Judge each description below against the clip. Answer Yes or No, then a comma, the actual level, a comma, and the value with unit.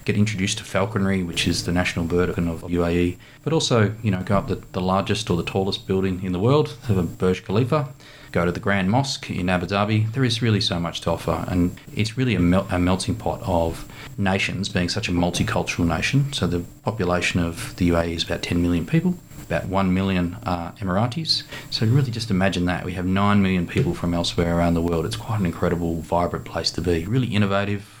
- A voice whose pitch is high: No, very low, 95 Hz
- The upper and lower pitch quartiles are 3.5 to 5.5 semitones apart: Yes, average, 4.2 semitones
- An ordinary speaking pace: No, fast, 215 wpm